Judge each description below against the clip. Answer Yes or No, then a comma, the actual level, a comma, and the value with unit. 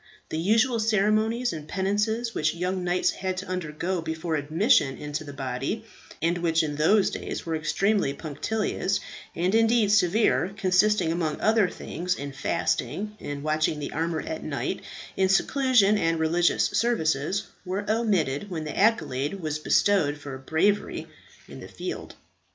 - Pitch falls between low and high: Yes, medium, 180 Hz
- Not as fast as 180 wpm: Yes, average, 150 wpm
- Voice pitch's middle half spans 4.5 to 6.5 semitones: Yes, average, 5.2 semitones